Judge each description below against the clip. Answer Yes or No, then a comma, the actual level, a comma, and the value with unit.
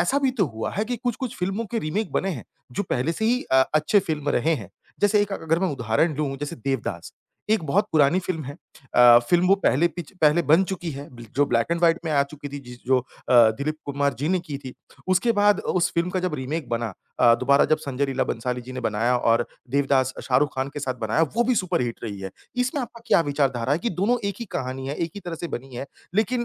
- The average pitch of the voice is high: No, medium, 150 Hz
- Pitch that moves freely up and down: Yes, wide, 6.2 semitones